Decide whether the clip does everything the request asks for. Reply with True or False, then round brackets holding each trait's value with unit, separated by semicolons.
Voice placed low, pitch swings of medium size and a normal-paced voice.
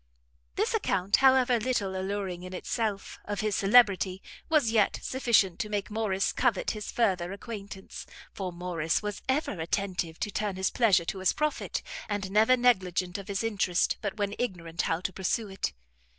False (200 Hz; 3.0 semitones; 165 wpm)